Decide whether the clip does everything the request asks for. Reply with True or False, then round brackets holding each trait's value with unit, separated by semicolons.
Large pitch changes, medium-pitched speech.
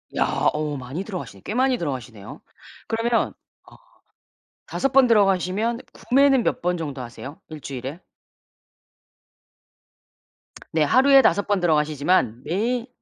True (8.1 semitones; 180 Hz)